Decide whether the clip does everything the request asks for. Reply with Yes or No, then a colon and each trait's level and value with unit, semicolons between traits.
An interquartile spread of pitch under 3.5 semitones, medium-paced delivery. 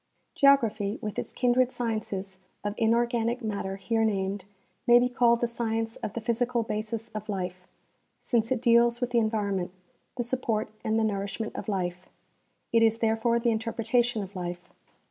Yes: narrow, 2.5 semitones; average, 165 wpm